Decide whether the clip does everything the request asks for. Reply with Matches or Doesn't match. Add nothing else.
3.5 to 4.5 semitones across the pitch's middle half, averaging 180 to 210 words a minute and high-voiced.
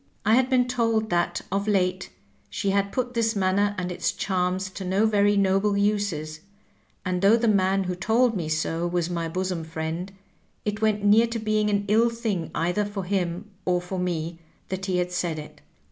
Doesn't match